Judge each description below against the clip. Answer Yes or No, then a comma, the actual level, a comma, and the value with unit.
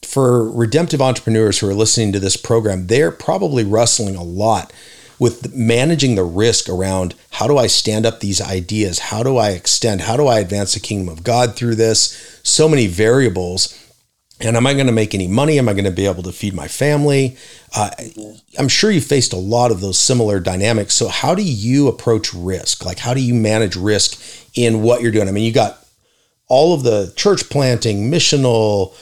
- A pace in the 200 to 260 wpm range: Yes, fast, 205 wpm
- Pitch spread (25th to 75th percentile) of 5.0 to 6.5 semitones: No, average, 3.6 semitones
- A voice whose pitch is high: No, low, 115 Hz